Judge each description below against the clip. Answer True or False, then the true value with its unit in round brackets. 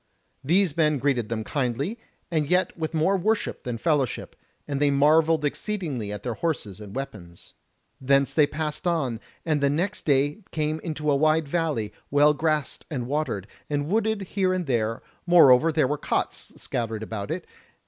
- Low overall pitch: False (150 Hz)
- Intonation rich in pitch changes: False (4.3 semitones)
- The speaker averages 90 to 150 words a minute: False (170 wpm)